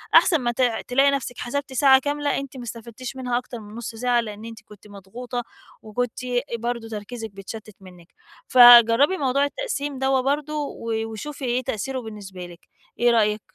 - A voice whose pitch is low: No, high, 240 Hz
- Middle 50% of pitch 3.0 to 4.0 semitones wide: Yes, average, 3.5 semitones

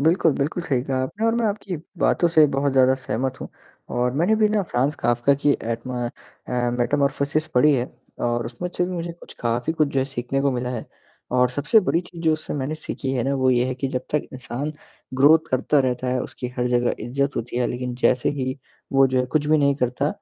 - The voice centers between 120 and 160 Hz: Yes, low, 135 Hz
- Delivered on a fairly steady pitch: No, average, 3.6 semitones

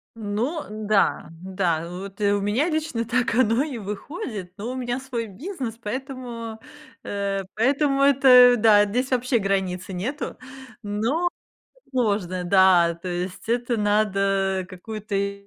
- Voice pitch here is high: Yes, high, 215 Hz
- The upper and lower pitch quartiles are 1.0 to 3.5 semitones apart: No, average, 4.2 semitones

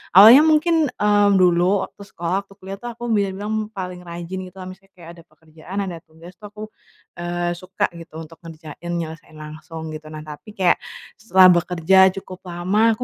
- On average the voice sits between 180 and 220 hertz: Yes, medium, 185 Hz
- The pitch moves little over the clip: No, average, 3.0 semitones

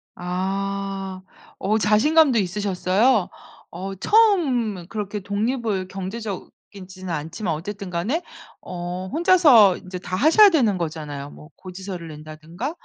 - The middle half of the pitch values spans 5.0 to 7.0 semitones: No, average, 3.9 semitones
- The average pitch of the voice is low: No, high, 195 Hz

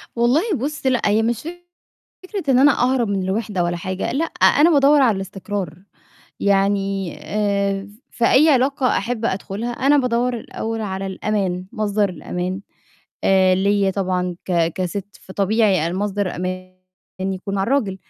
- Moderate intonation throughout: Yes, average, 4.2 semitones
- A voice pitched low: No, high, 200 Hz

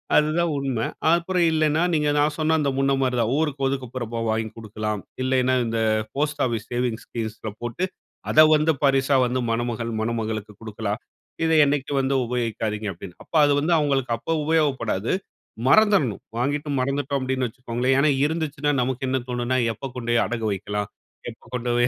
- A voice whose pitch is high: No, low, 130 Hz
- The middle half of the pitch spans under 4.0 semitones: No, average, 4.3 semitones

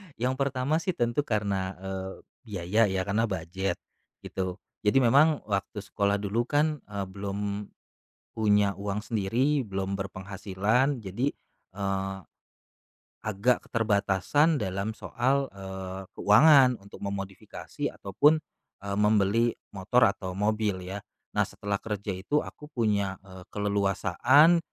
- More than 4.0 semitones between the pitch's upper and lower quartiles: No, average, 3.7 semitones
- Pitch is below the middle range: Yes, low, 100 Hz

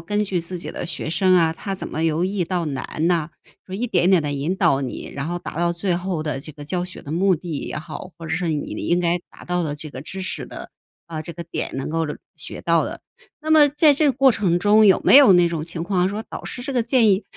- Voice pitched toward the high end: No, medium, 175 Hz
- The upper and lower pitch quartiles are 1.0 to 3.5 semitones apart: Yes, average, 3.2 semitones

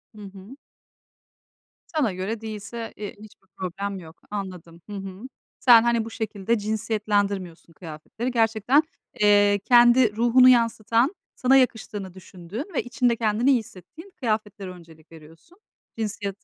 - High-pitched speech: Yes, high, 210 Hz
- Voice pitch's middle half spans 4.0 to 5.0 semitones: No, average, 3.5 semitones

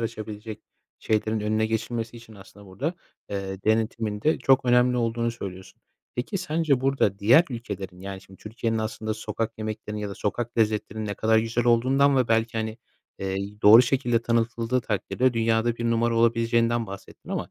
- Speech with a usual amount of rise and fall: No, narrow, 2.0 semitones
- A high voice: No, low, 115 Hz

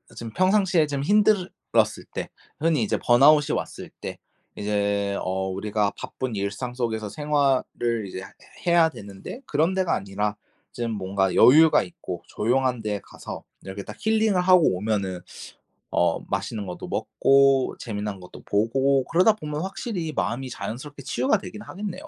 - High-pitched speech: No, low, 125 Hz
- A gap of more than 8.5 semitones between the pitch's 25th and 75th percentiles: No, wide, 7.5 semitones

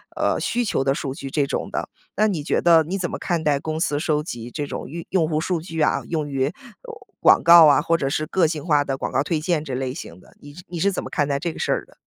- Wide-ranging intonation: No, average, 3.3 semitones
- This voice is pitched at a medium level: Yes, medium, 155 Hz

